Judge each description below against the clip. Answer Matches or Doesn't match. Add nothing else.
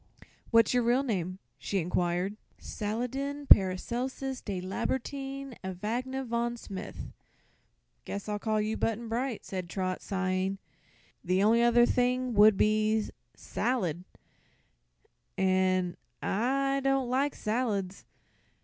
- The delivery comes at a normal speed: Doesn't match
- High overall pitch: Matches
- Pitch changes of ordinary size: Matches